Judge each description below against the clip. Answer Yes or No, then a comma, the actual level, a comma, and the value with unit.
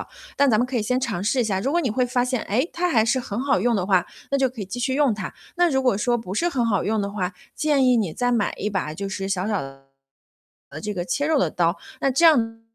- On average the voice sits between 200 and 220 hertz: No, high, 235 Hz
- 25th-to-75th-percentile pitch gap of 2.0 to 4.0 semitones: No, average, 4.9 semitones